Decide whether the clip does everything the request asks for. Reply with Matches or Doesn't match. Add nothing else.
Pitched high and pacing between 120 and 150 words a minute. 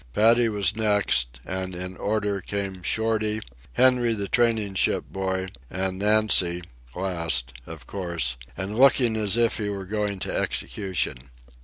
Doesn't match